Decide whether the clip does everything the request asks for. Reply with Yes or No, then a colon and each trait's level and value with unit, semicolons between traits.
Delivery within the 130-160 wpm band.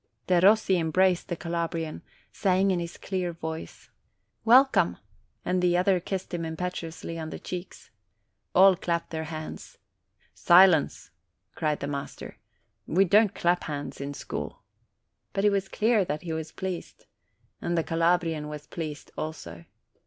Yes: average, 155 wpm